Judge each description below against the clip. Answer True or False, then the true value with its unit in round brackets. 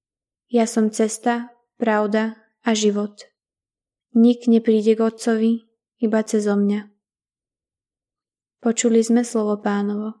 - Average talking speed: False (100 wpm)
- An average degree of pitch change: False (1.3 semitones)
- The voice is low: False (225 Hz)